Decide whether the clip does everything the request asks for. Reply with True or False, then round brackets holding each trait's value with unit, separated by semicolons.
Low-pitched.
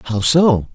True (130 Hz)